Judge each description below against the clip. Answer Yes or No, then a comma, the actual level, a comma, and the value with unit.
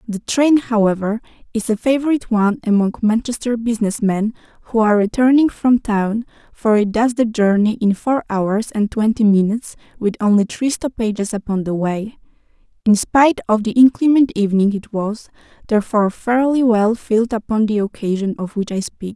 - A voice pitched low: No, high, 220 Hz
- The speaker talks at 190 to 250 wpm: No, average, 165 wpm